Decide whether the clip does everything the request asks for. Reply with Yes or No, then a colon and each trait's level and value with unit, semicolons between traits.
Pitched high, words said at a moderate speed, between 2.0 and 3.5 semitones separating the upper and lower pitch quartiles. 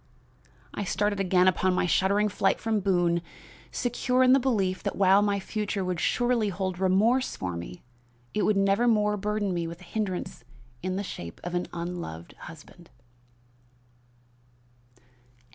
Yes: high, 195 Hz; average, 145 wpm; average, 2.9 semitones